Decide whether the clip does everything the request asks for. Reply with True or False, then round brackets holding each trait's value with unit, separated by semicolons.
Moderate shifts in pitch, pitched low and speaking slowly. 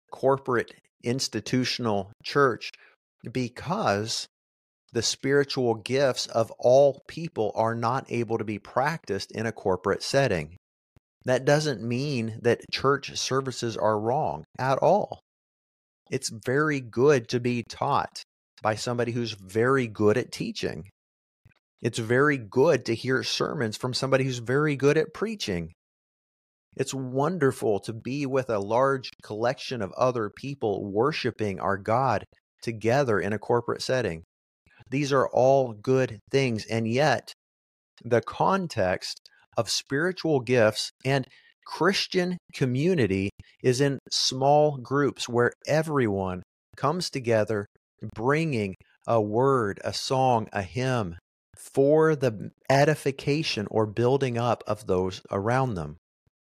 True (4.4 semitones; 120 Hz; 120 wpm)